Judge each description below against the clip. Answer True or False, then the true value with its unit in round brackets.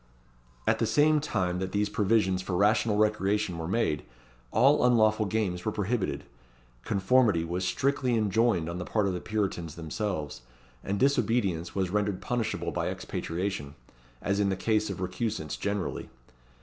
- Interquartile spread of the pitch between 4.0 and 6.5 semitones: False (3.4 semitones)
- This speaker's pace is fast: False (150 wpm)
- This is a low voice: True (100 Hz)